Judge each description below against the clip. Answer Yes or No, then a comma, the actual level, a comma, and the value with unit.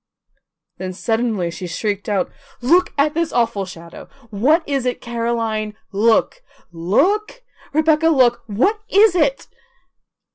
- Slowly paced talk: Yes, slow, 120 wpm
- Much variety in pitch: Yes, wide, 7.3 semitones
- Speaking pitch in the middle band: No, high, 235 Hz